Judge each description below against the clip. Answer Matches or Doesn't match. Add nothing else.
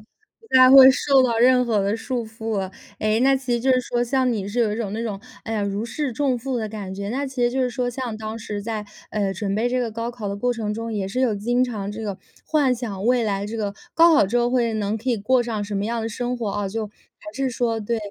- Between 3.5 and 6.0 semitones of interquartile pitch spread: Doesn't match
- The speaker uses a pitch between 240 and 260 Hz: Doesn't match